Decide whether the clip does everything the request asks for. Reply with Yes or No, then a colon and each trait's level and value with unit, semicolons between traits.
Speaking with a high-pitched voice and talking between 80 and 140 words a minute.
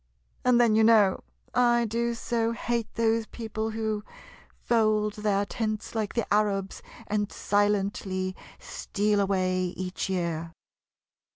Yes: high, 210 Hz; slow, 135 wpm